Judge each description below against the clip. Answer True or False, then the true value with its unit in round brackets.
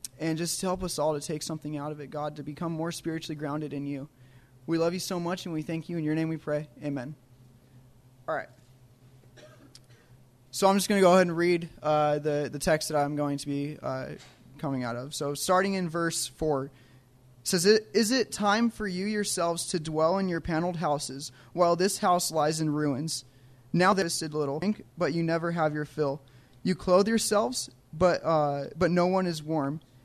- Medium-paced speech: False (215 wpm)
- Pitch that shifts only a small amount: False (4.5 semitones)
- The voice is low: False (155 Hz)